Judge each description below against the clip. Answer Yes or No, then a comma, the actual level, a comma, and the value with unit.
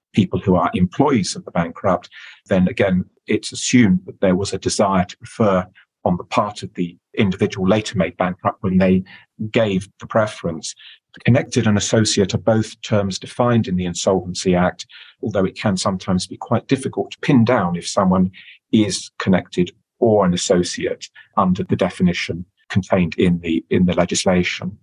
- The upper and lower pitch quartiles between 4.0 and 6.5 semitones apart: No, average, 3.3 semitones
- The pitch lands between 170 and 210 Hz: No, very low, 95 Hz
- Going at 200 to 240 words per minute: No, average, 165 wpm